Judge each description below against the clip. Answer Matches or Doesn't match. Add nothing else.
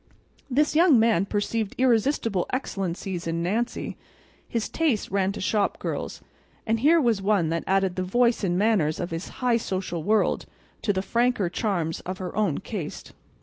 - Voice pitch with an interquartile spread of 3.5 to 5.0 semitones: Matches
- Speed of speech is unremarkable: Matches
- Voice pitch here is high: Matches